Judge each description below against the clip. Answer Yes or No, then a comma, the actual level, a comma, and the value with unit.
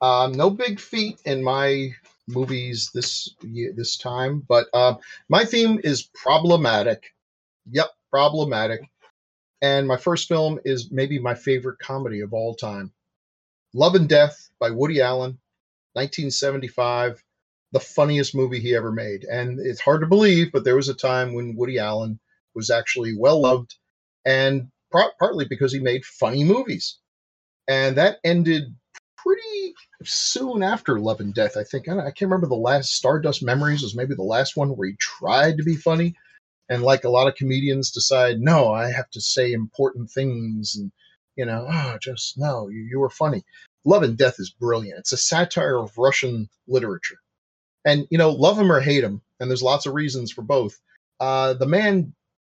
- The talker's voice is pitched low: Yes, low, 130 Hz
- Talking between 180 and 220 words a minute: No, average, 170 wpm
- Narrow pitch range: No, average, 3.8 semitones